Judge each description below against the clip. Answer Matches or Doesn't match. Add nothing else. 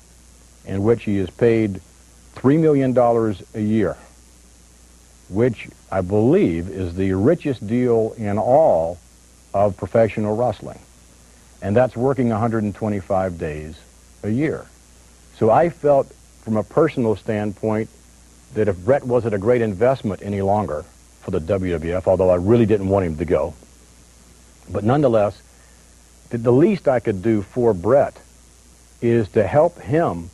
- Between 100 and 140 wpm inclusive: Matches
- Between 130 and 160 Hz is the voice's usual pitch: Doesn't match